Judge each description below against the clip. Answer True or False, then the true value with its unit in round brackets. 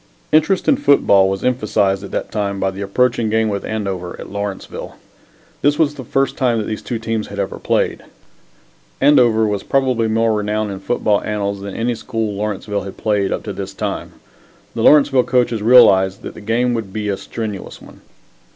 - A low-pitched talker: True (110 Hz)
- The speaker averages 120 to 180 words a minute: False (190 wpm)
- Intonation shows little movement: False (3.4 semitones)